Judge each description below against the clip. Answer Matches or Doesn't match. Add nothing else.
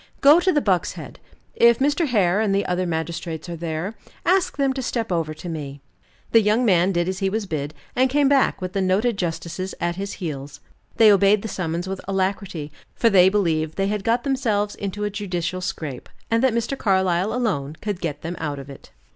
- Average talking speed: Doesn't match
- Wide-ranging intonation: Doesn't match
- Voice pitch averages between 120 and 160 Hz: Doesn't match